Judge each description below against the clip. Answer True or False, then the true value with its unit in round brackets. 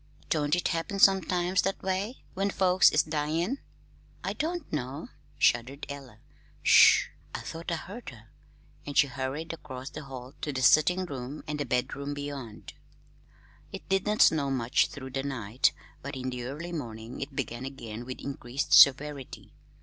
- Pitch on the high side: False (140 Hz)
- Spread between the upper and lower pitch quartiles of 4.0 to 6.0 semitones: True (4.6 semitones)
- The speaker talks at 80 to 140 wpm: False (165 wpm)